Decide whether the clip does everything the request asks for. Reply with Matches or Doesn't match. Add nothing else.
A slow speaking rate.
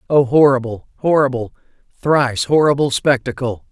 Matches